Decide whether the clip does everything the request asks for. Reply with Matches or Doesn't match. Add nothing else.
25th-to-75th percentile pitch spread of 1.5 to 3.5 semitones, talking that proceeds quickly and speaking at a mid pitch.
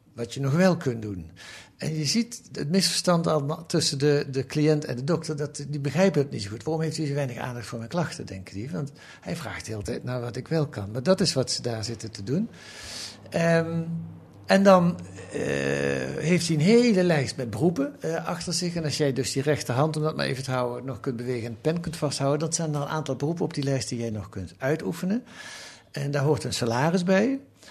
Doesn't match